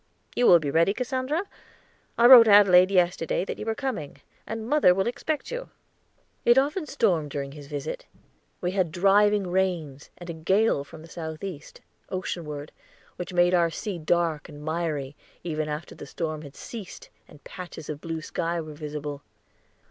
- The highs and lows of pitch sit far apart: No, average, 4.9 semitones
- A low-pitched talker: No, medium, 175 Hz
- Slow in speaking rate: No, average, 165 wpm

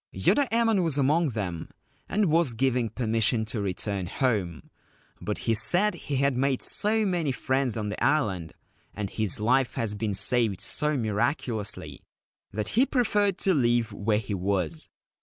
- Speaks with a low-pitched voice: Yes, low, 120 Hz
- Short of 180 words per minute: Yes, average, 160 wpm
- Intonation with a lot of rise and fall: Yes, wide, 6.5 semitones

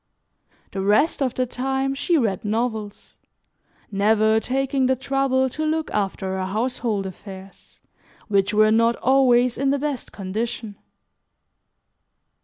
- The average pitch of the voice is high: Yes, high, 235 Hz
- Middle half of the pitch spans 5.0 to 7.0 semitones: No, average, 4.4 semitones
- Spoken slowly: Yes, slow, 125 wpm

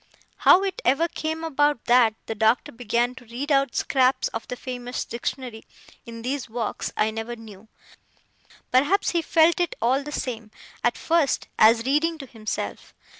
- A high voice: Yes, very high, 250 Hz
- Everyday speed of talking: Yes, average, 165 wpm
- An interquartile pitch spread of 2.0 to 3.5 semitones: No, average, 4.4 semitones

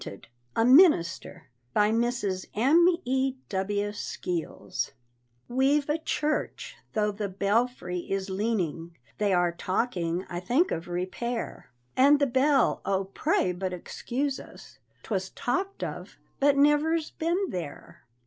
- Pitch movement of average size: No, wide, 6.9 semitones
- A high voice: Yes, high, 220 Hz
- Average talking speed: No, slow, 120 wpm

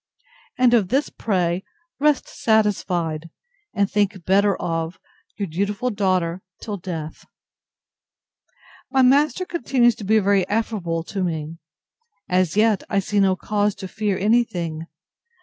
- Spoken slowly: Yes, slow, 130 wpm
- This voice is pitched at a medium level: No, high, 200 Hz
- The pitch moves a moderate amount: Yes, average, 3.7 semitones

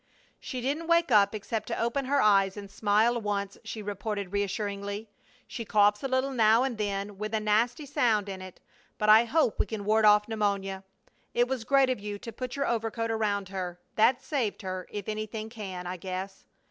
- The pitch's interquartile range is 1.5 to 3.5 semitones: Yes, average, 2.8 semitones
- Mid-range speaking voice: No, high, 215 Hz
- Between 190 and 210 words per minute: Yes, average, 200 wpm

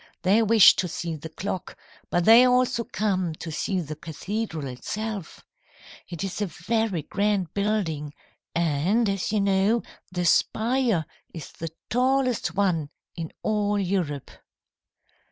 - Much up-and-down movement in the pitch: No, average, 4.8 semitones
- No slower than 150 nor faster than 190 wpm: No, slow, 135 wpm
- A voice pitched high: Yes, high, 195 Hz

